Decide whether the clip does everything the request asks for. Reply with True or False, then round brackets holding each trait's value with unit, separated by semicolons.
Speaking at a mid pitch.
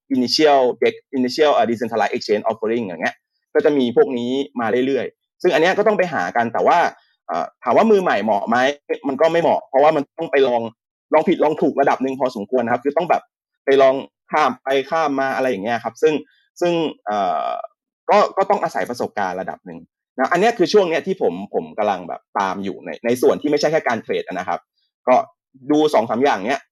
True (155 Hz)